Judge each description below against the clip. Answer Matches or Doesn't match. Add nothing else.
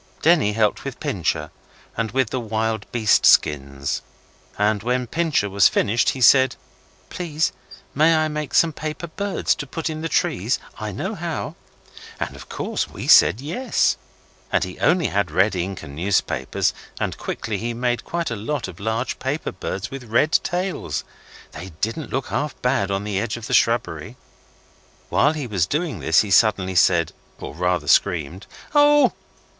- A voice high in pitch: Doesn't match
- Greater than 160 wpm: Matches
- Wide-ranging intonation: Matches